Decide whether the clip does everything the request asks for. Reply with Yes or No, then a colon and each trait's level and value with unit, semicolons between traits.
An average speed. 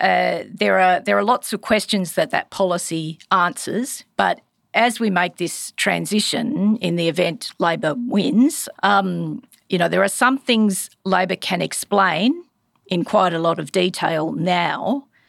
Yes: average, 155 wpm